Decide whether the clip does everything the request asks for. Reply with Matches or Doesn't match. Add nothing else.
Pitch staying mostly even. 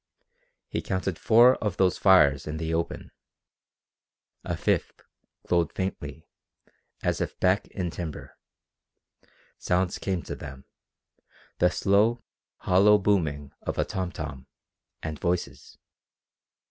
Doesn't match